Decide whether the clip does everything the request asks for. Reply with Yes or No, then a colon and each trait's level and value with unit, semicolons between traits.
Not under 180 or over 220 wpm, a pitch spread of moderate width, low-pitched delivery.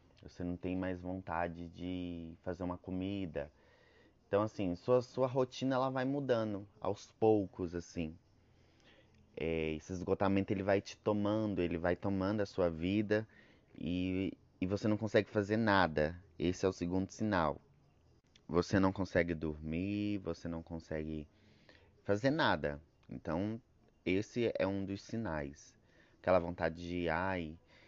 No: average, 140 wpm; average, 3.5 semitones; very low, 95 Hz